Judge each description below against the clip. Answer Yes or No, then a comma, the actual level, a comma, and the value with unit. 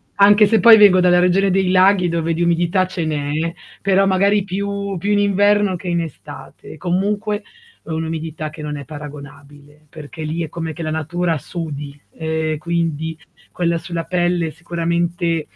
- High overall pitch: No, medium, 170 Hz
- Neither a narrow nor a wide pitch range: Yes, average, 3.1 semitones